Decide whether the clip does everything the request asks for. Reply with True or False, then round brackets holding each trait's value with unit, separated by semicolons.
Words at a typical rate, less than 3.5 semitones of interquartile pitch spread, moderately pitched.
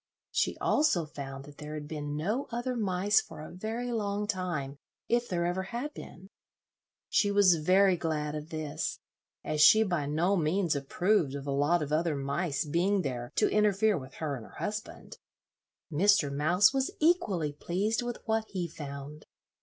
False (170 wpm; 5.5 semitones; 175 Hz)